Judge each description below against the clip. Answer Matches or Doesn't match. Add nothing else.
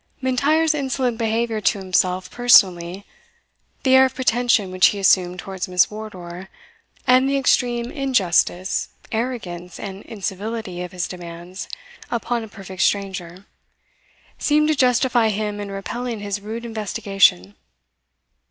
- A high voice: Matches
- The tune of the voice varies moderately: Matches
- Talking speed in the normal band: Doesn't match